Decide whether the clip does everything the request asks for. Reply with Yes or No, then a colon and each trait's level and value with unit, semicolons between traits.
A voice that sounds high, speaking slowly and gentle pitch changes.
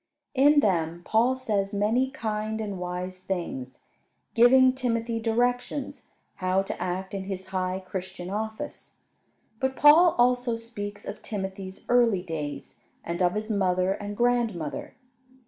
No: high, 205 Hz; slow, 130 wpm; average, 4.5 semitones